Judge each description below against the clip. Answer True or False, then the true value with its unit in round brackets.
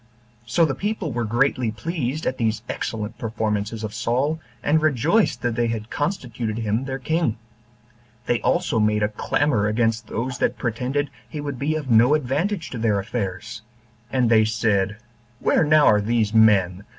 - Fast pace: False (165 wpm)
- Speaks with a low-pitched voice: True (120 Hz)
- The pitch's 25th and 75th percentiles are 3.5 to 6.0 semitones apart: True (4.7 semitones)